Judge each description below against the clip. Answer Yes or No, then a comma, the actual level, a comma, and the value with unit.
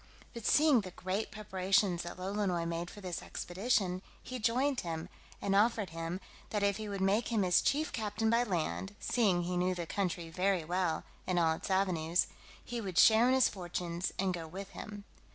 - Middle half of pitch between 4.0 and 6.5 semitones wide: No, average, 3.3 semitones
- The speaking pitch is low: No, high, 190 Hz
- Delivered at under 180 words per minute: No, average, 190 wpm